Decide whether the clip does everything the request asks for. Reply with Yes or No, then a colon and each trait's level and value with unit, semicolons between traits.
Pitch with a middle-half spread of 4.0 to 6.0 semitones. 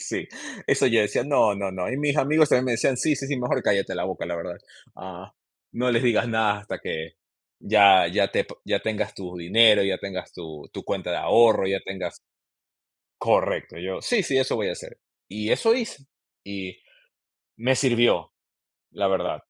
Yes: average, 5.0 semitones